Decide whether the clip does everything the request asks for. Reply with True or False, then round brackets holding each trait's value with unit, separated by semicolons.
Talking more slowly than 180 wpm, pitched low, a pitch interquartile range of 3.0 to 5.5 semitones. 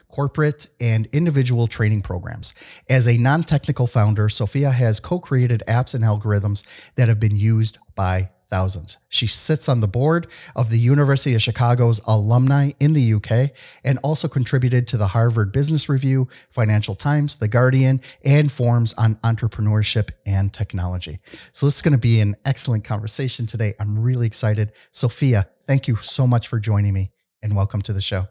True (165 wpm; 115 Hz; 4.0 semitones)